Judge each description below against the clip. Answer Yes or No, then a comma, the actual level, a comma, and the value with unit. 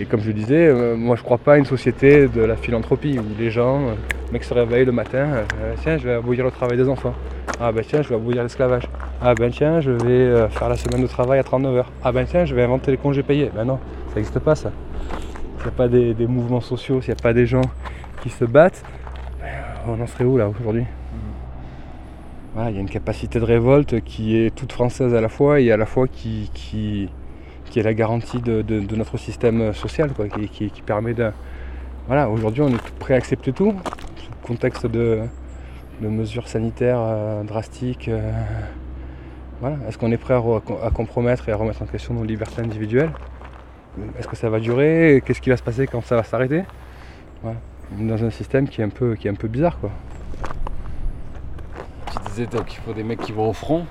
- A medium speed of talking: No, fast, 235 wpm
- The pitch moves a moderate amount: Yes, average, 3.0 semitones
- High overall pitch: No, low, 115 Hz